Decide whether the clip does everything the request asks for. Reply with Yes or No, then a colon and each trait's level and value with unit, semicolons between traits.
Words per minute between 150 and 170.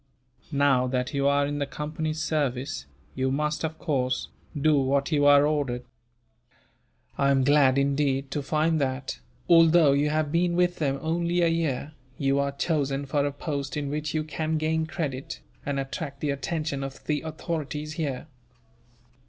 Yes: average, 165 wpm